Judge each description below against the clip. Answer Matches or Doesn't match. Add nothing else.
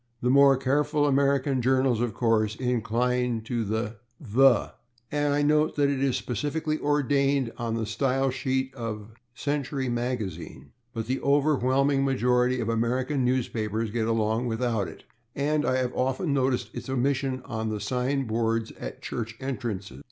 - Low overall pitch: Matches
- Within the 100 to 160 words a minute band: Matches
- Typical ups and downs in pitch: Matches